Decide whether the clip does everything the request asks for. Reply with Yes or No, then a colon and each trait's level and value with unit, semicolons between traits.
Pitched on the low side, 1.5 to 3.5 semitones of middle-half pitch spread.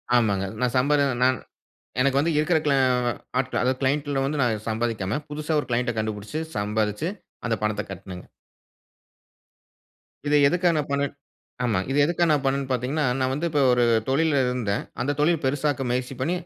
No: low, 130 Hz; average, 4.2 semitones